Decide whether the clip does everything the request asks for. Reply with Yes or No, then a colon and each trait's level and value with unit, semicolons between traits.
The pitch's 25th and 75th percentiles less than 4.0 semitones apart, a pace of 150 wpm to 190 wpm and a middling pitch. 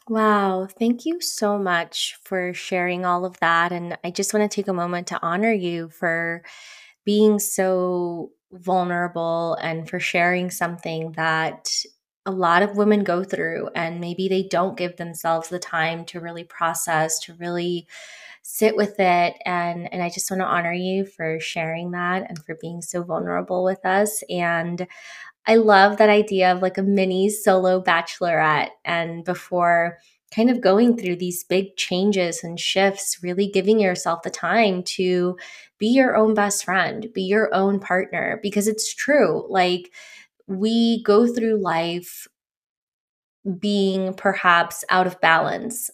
Yes: average, 2.9 semitones; average, 155 wpm; medium, 180 Hz